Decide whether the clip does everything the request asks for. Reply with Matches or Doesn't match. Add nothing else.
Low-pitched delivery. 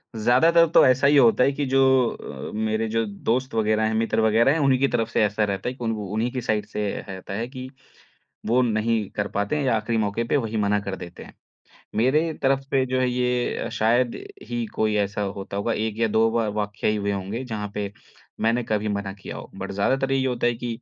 Matches